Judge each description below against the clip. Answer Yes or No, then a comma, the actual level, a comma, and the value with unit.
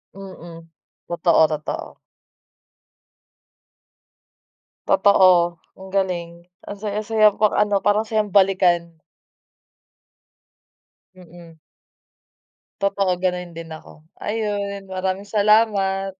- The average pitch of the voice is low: No, high, 190 Hz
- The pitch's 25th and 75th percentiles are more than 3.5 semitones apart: No, average, 2.9 semitones